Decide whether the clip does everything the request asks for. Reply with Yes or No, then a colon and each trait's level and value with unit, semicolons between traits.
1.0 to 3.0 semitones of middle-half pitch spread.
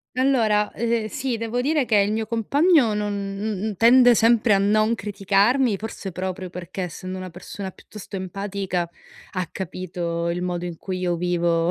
No: average, 3.9 semitones